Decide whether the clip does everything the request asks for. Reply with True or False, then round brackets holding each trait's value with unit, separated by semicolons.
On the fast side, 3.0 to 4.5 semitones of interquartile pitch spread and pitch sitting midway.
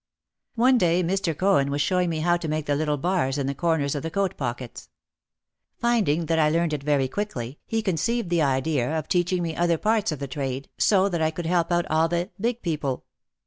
True (220 wpm; 4.0 semitones; 165 Hz)